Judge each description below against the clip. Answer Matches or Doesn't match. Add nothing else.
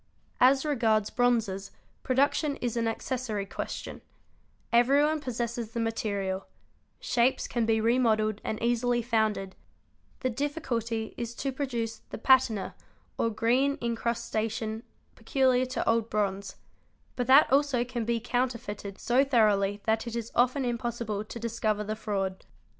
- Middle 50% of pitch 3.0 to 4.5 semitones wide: Doesn't match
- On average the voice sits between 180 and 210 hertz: Doesn't match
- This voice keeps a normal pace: Doesn't match